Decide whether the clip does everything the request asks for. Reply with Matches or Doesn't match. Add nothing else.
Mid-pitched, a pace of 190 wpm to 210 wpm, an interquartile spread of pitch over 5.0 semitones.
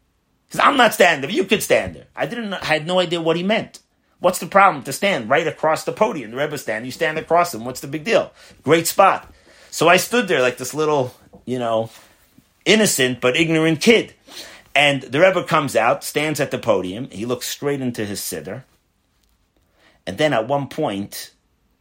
Matches